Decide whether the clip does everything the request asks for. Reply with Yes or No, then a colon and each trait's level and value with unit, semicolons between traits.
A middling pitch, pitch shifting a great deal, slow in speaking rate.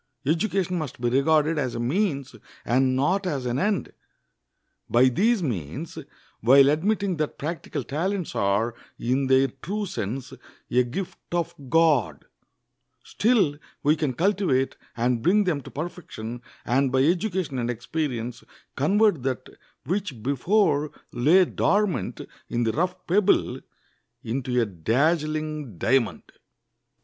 Yes: medium, 145 Hz; wide, 6.1 semitones; slow, 125 wpm